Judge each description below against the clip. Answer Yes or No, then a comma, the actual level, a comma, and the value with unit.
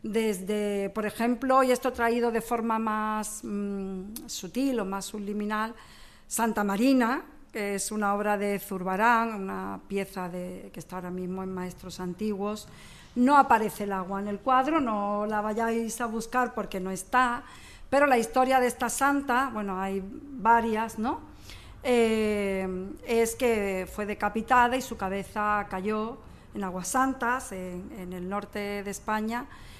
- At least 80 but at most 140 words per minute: No, average, 150 wpm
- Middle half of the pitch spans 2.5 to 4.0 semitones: Yes, average, 3.3 semitones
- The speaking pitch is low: No, high, 215 Hz